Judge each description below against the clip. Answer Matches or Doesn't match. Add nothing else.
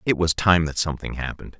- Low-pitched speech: Matches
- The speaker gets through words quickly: Matches